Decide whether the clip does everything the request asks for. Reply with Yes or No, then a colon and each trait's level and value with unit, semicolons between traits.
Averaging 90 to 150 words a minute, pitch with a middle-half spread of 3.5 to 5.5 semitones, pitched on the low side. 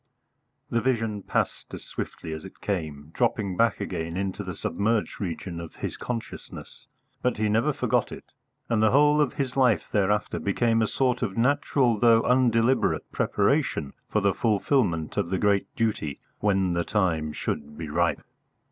No: average, 165 wpm; average, 4.6 semitones; low, 105 Hz